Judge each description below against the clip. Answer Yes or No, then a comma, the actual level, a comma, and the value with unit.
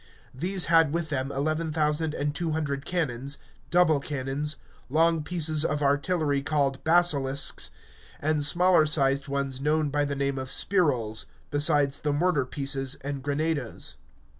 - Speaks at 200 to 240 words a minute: No, average, 140 wpm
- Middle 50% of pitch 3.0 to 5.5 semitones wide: No, narrow, 2.4 semitones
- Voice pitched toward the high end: No, medium, 145 Hz